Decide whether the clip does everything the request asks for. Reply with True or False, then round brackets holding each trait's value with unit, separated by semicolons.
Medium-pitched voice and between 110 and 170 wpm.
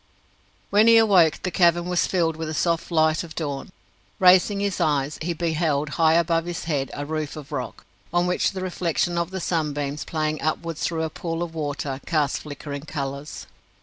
False (160 Hz; 185 wpm)